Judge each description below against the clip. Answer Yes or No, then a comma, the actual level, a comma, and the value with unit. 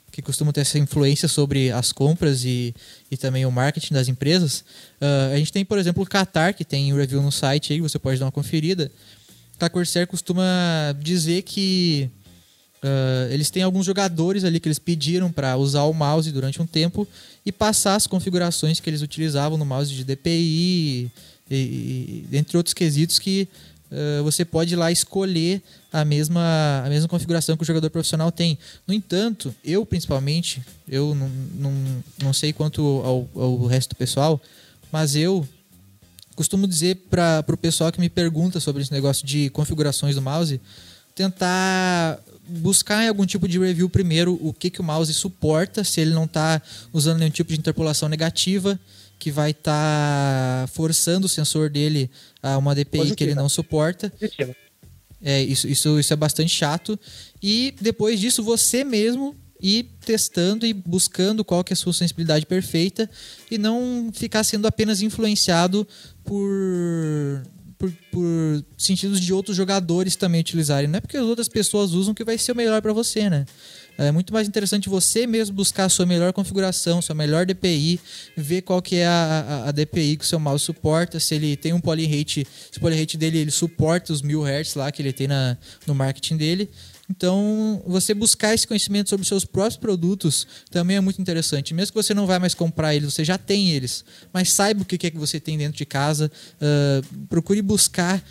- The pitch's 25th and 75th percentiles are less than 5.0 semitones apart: Yes, average, 4.4 semitones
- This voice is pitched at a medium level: Yes, medium, 165 Hz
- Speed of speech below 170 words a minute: No, fast, 185 wpm